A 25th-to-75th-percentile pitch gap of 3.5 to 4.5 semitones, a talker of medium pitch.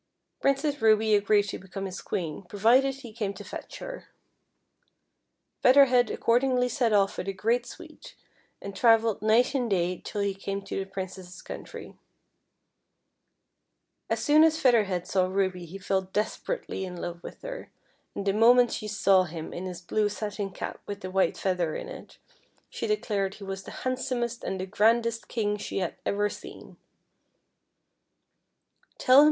No: average, 4.0 semitones; high, 205 Hz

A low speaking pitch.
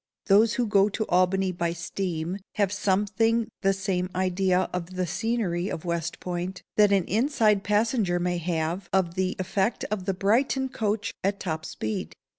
No: high, 190 Hz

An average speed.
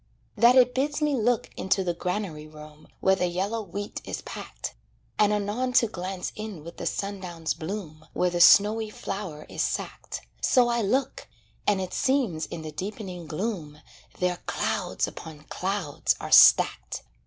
Yes: average, 160 wpm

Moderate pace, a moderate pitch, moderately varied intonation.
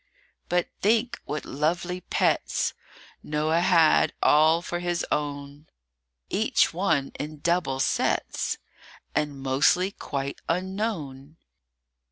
No: slow, 100 wpm; medium, 155 Hz; average, 3.7 semitones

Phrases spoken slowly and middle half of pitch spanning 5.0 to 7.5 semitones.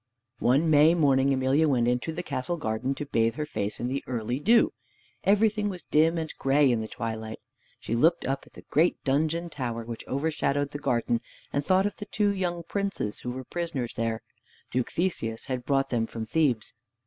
No: average, 195 wpm; wide, 5.5 semitones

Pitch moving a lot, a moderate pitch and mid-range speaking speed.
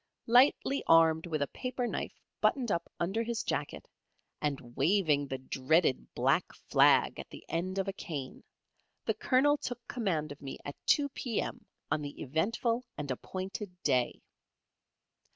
Yes: wide, 8.3 semitones; medium, 175 Hz; average, 150 wpm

